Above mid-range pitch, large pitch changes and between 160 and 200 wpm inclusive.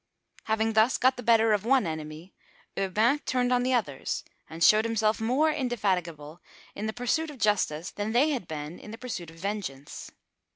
Yes: high, 215 Hz; wide, 6.0 semitones; average, 180 wpm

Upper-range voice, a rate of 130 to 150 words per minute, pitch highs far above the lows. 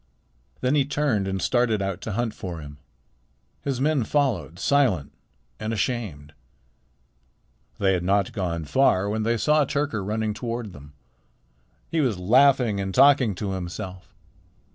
No: low, 110 Hz; average, 140 wpm; wide, 5.7 semitones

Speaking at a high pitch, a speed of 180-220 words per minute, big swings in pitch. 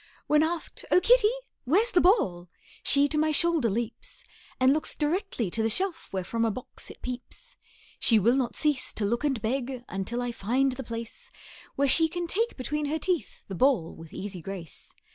Yes: very high, 260 Hz; average, 195 wpm; wide, 6.1 semitones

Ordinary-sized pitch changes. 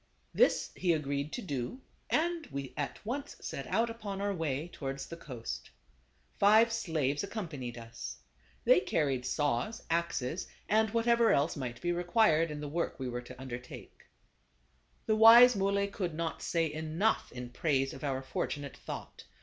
No: wide, 7.8 semitones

